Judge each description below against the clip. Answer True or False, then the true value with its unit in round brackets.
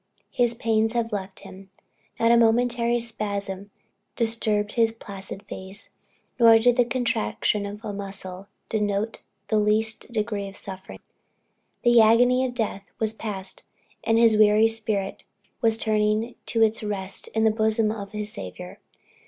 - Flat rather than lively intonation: True (2.2 semitones)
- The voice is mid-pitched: False (215 Hz)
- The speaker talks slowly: False (145 wpm)